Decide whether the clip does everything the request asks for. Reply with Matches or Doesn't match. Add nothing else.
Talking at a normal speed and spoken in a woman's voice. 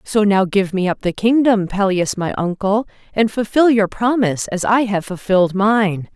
Matches